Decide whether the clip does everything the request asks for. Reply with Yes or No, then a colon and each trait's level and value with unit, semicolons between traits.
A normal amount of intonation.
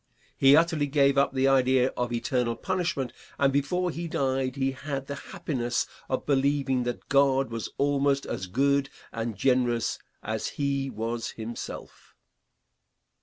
No: narrow, 2.3 semitones